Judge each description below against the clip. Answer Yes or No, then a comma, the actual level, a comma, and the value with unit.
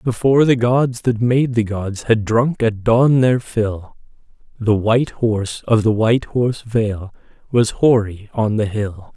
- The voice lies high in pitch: No, low, 115 Hz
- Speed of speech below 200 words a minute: Yes, average, 170 wpm